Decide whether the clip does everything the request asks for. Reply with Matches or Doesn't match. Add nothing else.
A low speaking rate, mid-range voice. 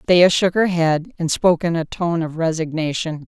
Doesn't match